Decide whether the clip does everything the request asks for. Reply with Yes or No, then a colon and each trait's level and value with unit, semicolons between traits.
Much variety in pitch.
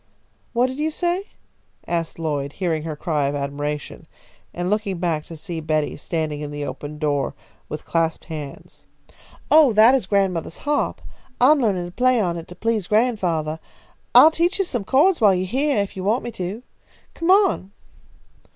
Yes: wide, 7.9 semitones